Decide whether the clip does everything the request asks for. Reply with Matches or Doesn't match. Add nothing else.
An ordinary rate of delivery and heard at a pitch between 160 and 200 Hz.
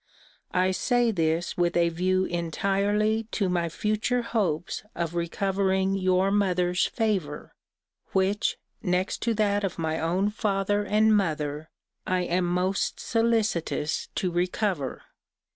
Doesn't match